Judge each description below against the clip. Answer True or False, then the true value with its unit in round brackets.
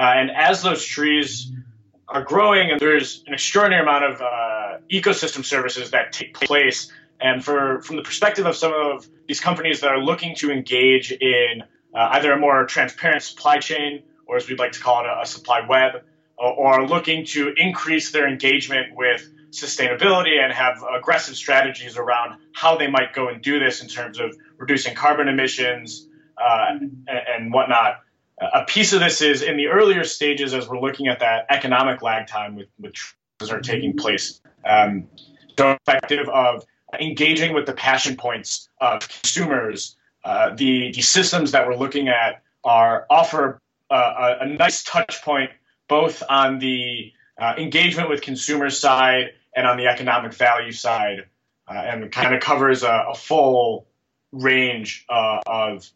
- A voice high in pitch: False (135 Hz)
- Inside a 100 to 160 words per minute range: False (170 wpm)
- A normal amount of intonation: True (3.7 semitones)